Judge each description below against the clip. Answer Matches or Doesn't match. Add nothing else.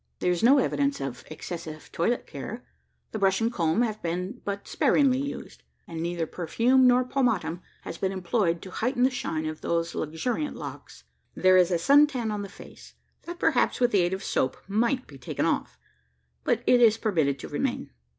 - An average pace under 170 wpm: Doesn't match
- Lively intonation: Matches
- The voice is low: Doesn't match